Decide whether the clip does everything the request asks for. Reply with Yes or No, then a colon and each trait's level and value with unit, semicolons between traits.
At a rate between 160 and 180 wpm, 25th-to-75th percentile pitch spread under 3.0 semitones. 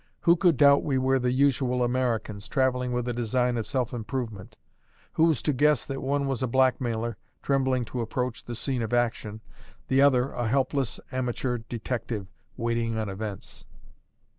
Yes: average, 165 wpm; narrow, 2.4 semitones